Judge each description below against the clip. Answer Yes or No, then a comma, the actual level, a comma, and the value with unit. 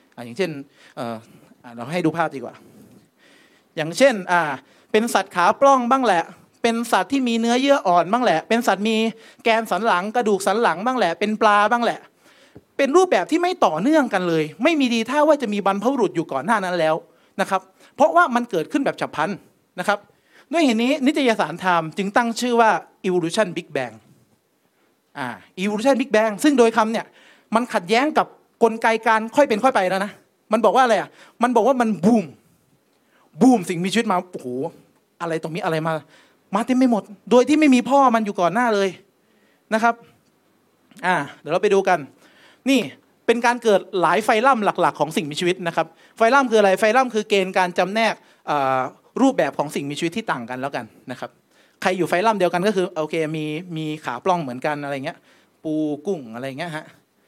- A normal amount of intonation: No, wide, 5.8 semitones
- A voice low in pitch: No, high, 205 Hz